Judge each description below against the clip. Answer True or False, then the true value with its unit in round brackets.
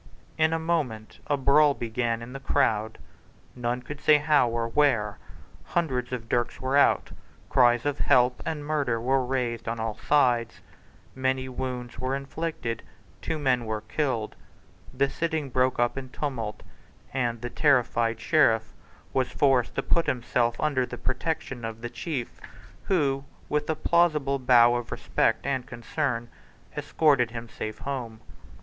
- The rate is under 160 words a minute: True (150 wpm)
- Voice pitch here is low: True (130 Hz)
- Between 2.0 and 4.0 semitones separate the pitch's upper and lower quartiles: True (3.4 semitones)